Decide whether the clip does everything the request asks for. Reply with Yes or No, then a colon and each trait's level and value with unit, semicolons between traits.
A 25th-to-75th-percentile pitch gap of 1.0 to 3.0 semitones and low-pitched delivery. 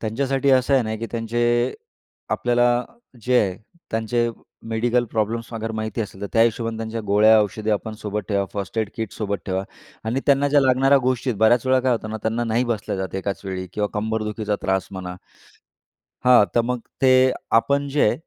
Yes: narrow, 2.6 semitones; low, 115 Hz